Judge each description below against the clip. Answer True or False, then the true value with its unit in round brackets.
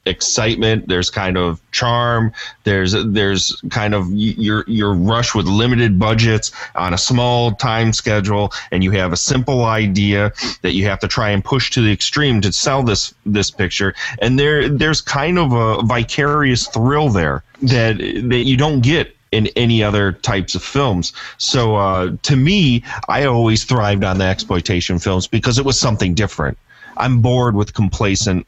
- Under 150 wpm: False (170 wpm)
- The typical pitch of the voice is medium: False (110 Hz)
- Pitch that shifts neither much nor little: True (3.9 semitones)